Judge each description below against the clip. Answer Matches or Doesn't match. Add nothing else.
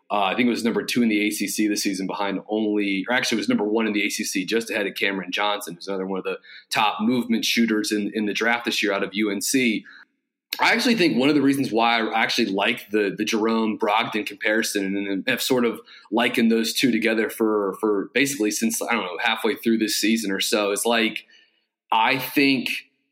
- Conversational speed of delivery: Doesn't match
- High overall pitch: Doesn't match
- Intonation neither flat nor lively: Doesn't match